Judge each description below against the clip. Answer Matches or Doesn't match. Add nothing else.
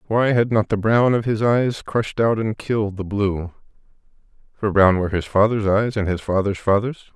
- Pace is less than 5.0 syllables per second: Doesn't match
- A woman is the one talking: Doesn't match